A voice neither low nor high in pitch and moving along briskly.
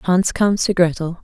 No: medium, 180 Hz; average, 195 wpm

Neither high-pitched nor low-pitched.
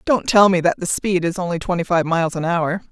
Yes: medium, 175 Hz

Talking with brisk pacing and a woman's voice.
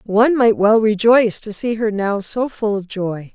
Yes: fast, 215 wpm; female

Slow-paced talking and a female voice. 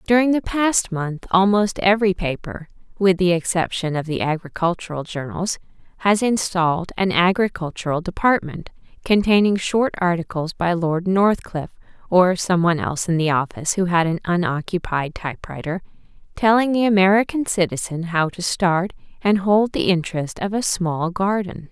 No: average, 145 wpm; female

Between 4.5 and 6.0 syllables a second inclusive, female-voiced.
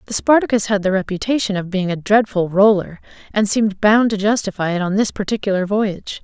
Yes: 5.9 syllables/s; female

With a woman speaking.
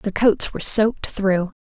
Yes: female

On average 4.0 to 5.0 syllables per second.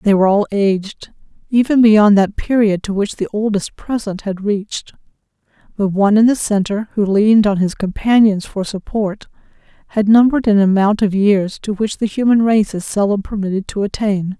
No: 5.2 syllables/s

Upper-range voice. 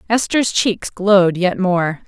Yes: high, 195 Hz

